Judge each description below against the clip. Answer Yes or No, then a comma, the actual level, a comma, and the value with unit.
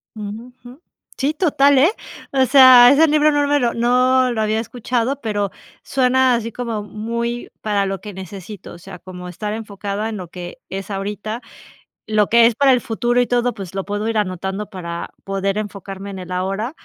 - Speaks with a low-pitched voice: No, high, 220 Hz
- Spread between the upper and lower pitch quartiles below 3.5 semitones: No, average, 4.0 semitones